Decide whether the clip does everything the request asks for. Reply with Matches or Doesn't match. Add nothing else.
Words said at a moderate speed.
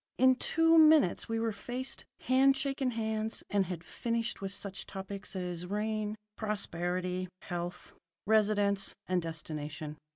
Doesn't match